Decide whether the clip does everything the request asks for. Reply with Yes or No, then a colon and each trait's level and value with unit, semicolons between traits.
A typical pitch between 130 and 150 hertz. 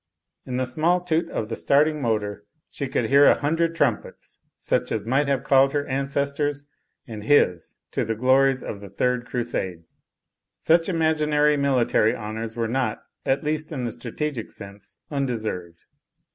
Yes: low, 135 Hz